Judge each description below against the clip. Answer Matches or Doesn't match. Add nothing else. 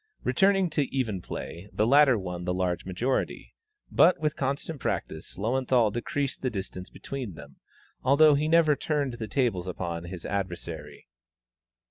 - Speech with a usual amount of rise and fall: Doesn't match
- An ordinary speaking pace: Matches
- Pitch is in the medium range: Doesn't match